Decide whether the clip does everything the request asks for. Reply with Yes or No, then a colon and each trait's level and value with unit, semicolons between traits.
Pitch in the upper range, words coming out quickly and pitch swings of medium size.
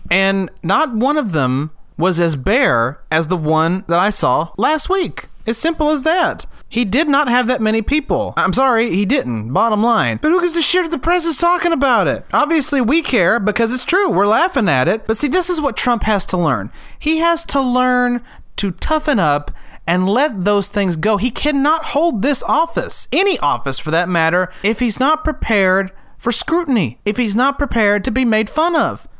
No: high, 240 Hz; fast, 210 wpm; wide, 8.0 semitones